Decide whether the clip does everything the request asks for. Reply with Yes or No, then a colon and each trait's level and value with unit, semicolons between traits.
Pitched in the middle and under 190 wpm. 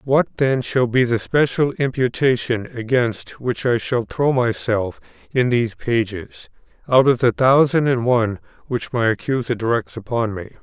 No: low, 120 Hz; average, 160 wpm